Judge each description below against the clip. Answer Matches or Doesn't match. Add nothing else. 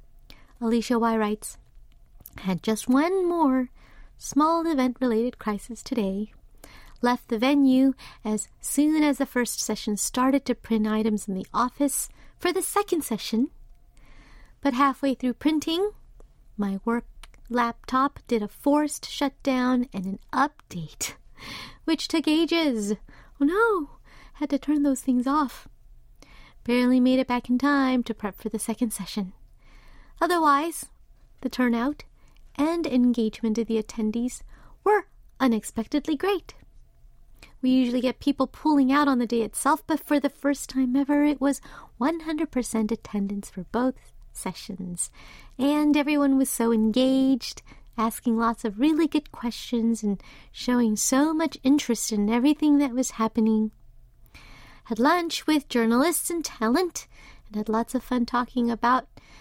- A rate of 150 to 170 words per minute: Doesn't match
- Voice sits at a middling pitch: Doesn't match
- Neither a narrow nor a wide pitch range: Matches